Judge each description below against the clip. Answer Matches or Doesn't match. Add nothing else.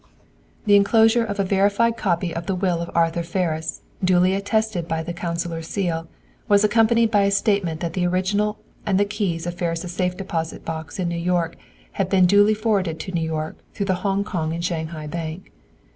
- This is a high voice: Doesn't match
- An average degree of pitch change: Matches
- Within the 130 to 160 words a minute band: Doesn't match